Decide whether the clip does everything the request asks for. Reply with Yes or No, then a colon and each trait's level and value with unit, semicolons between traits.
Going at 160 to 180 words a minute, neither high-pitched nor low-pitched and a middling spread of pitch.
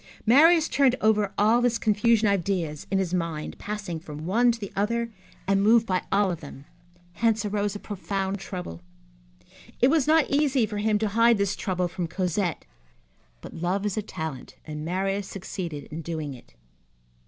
No: average, 175 wpm; high, 200 Hz; average, 4.2 semitones